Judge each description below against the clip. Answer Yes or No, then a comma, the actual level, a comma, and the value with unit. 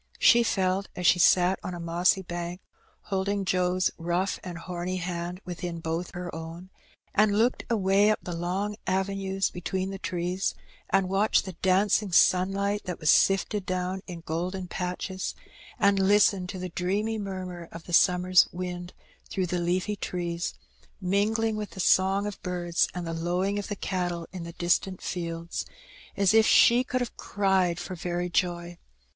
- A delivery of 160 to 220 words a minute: Yes, average, 165 wpm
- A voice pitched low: No, medium, 185 Hz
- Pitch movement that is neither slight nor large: No, narrow, 1.9 semitones